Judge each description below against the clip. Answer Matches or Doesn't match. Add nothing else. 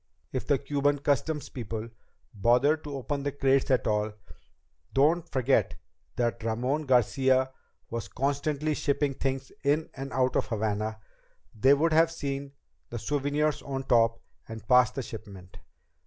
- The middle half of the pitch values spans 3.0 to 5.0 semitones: Matches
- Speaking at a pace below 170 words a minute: Matches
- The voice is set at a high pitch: Doesn't match